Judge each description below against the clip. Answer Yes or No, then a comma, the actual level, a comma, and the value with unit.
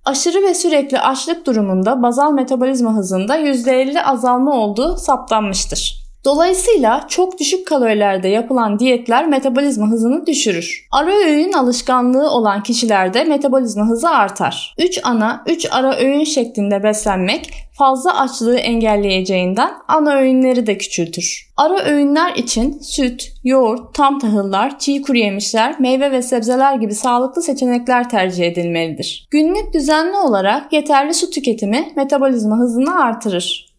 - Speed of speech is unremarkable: Yes, average, 125 wpm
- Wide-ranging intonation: No, average, 4.7 semitones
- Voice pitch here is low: No, very high, 260 Hz